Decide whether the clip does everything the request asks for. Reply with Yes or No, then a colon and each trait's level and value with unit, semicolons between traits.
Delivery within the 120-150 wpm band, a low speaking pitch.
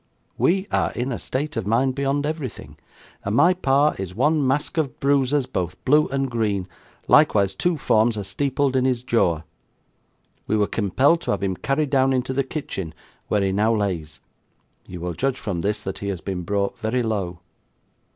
No: average, 185 wpm; low, 120 Hz